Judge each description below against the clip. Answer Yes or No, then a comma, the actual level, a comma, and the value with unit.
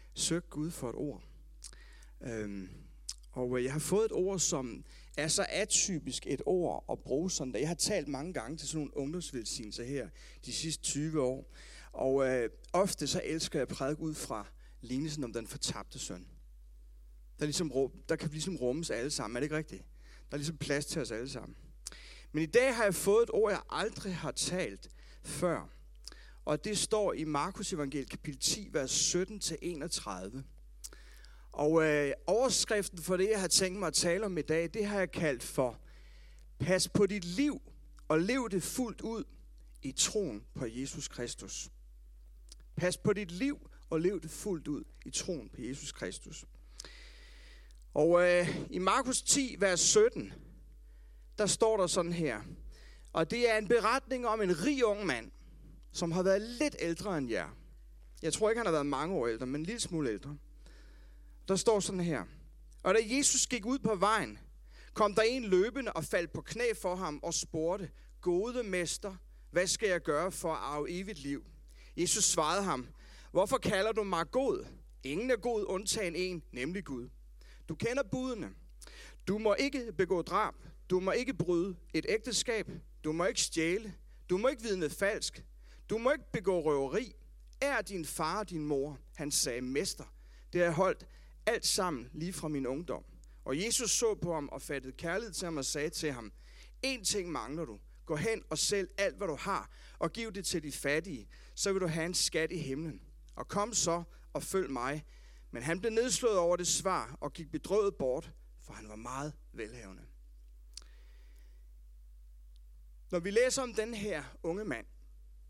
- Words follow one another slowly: No, average, 180 wpm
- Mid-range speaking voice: Yes, medium, 165 Hz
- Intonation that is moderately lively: No, wide, 6.8 semitones